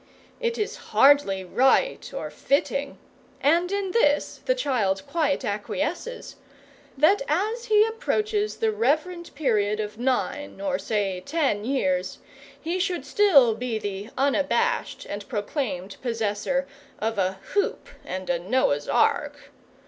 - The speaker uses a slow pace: Yes, slow, 125 wpm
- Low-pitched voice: No, very high, 275 Hz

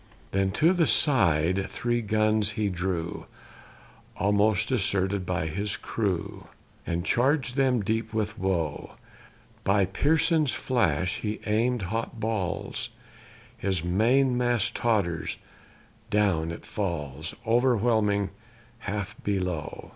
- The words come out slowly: Yes, slow, 110 wpm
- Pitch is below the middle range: Yes, low, 105 Hz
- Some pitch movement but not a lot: Yes, average, 4.2 semitones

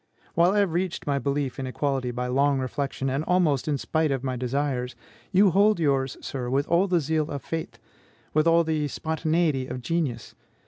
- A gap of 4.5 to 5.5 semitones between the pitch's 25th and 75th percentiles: No, average, 3.9 semitones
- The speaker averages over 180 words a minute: Yes, average, 190 wpm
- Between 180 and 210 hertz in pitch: No, medium, 145 Hz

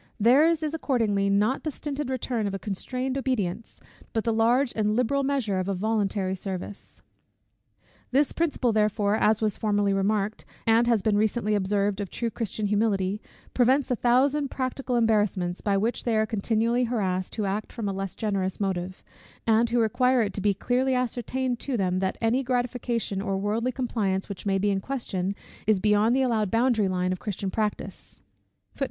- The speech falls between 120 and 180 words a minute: Yes, average, 175 wpm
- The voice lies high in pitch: Yes, high, 220 Hz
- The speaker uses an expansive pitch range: No, average, 3.8 semitones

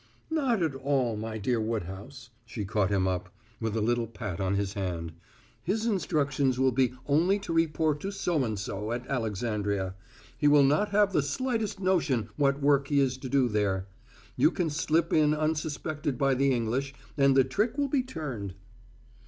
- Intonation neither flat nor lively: No, wide, 6.2 semitones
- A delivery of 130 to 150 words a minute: No, average, 180 wpm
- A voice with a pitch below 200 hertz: Yes, low, 135 Hz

